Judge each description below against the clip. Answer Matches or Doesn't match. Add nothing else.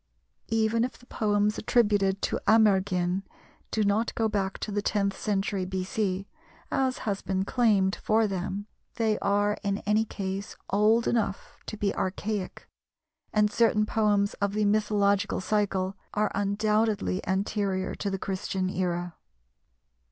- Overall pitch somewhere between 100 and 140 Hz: Doesn't match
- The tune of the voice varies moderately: Doesn't match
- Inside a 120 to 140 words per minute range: Matches